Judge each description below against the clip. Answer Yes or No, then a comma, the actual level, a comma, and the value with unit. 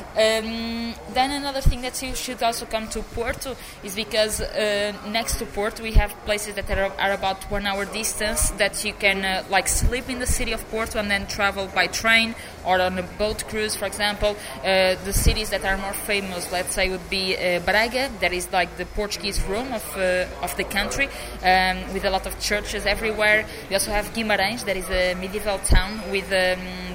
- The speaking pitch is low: No, high, 205 Hz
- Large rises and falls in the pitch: No, narrow, 2.5 semitones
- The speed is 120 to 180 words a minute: No, fast, 205 wpm